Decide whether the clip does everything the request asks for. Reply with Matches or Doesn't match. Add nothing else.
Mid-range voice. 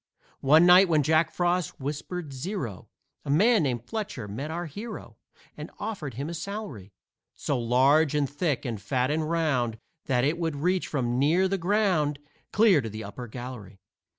Matches